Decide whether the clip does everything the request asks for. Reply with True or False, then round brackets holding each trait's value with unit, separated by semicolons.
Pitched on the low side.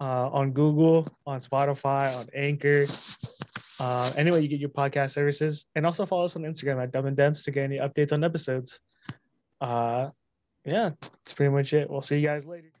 False (145 Hz)